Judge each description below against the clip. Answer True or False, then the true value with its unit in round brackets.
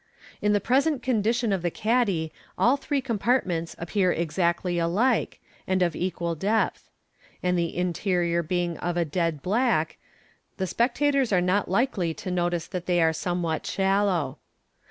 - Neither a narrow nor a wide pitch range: True (4.5 semitones)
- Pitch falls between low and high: True (180 Hz)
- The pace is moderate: True (155 wpm)